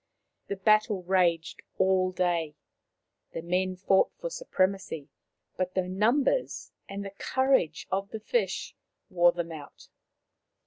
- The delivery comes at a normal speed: No, slow, 125 wpm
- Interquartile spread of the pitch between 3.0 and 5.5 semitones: No, narrow, 2.4 semitones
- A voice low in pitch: No, medium, 185 Hz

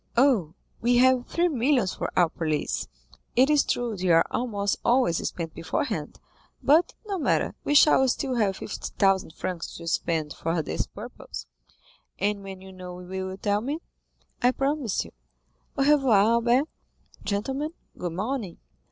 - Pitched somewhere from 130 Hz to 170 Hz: No, high, 210 Hz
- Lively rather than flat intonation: Yes, wide, 6.4 semitones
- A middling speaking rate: Yes, average, 155 wpm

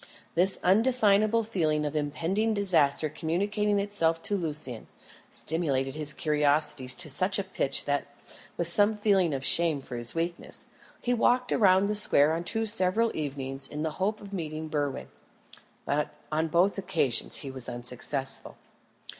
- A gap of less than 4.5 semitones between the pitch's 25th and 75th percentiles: No, wide, 5.5 semitones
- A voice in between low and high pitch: Yes, medium, 165 Hz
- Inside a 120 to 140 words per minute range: No, average, 150 wpm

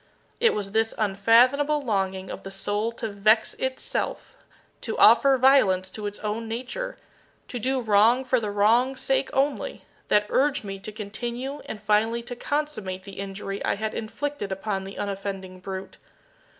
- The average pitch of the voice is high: Yes, high, 215 Hz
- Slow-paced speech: No, average, 160 wpm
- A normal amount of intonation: Yes, average, 4.5 semitones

